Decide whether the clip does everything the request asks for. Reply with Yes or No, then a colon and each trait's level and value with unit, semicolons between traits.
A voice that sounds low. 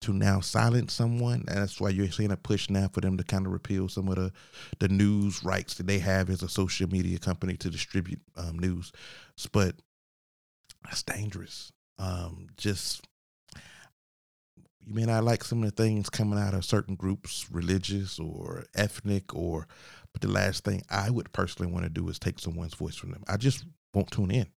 Yes: very low, 95 Hz